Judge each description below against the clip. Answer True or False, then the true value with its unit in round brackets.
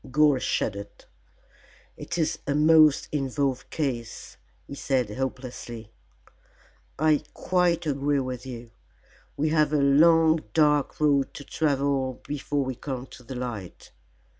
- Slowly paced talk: True (125 wpm)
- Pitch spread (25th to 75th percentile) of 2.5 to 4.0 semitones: True (3.0 semitones)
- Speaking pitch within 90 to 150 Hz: True (140 Hz)